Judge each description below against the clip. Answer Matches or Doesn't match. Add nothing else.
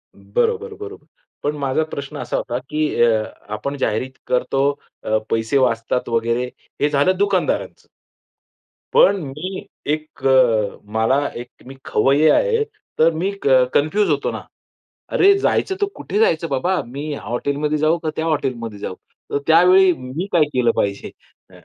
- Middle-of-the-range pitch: Matches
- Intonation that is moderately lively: Doesn't match